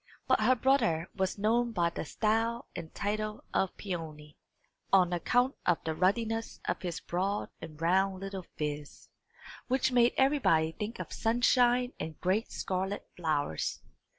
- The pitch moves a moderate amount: No, wide, 5.7 semitones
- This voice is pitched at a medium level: No, high, 195 Hz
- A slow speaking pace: No, average, 145 wpm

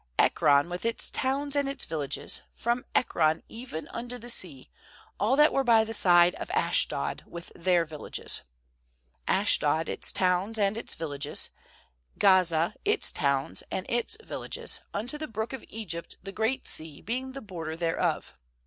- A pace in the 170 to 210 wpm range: No, average, 160 wpm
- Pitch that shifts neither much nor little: No, wide, 6.6 semitones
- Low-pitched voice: No, high, 195 Hz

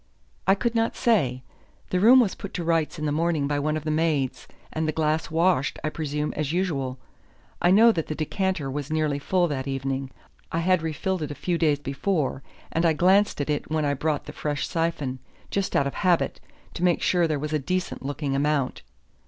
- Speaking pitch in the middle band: Yes, medium, 155 Hz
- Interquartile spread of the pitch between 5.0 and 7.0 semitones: No, average, 3.6 semitones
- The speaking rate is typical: No, fast, 210 wpm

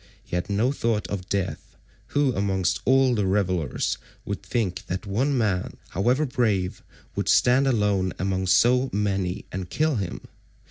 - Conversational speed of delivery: Yes, average, 145 wpm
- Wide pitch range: No, average, 4.9 semitones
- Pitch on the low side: Yes, low, 100 Hz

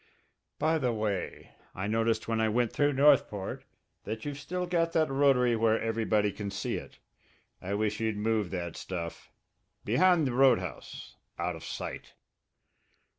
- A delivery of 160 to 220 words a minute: No, average, 150 wpm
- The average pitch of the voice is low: Yes, low, 115 Hz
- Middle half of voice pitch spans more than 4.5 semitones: Yes, average, 5.1 semitones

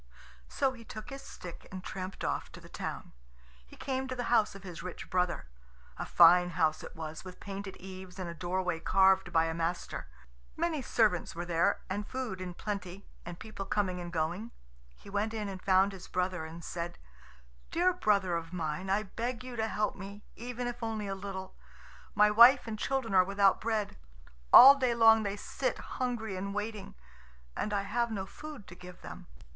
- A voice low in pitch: No, high, 195 Hz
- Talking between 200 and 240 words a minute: No, average, 190 wpm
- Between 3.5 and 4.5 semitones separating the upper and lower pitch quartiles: Yes, average, 3.8 semitones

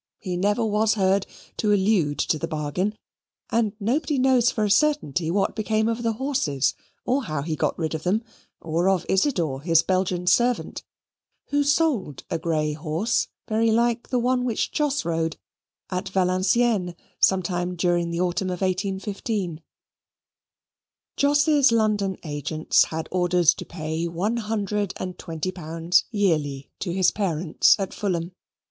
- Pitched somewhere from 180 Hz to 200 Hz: Yes, high, 190 Hz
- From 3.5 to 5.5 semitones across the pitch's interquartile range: Yes, average, 4.9 semitones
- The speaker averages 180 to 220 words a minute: No, average, 150 wpm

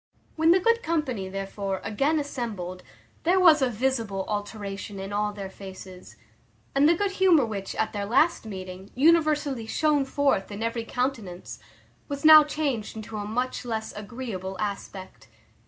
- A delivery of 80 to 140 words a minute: No, average, 155 wpm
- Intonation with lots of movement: Yes, wide, 6.5 semitones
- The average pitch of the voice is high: Yes, high, 225 Hz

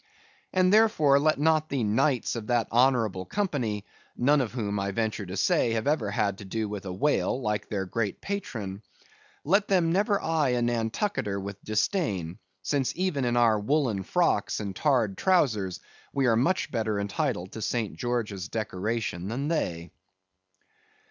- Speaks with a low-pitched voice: Yes, low, 115 Hz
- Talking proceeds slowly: No, average, 160 wpm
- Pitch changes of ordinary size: No, wide, 6.3 semitones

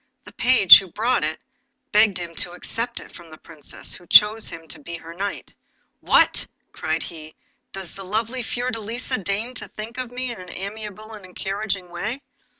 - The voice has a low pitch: No, high, 205 Hz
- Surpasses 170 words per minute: Yes, average, 185 wpm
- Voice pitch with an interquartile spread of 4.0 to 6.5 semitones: Yes, average, 4.4 semitones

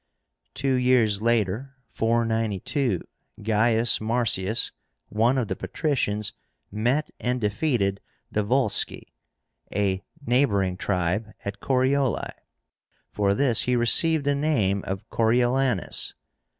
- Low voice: Yes, low, 115 Hz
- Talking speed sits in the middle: No, slow, 100 wpm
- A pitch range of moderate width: Yes, average, 3.9 semitones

